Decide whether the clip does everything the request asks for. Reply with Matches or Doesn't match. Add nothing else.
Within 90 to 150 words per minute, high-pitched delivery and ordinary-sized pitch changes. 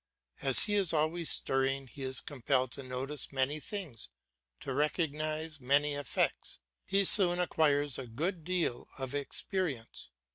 Doesn't match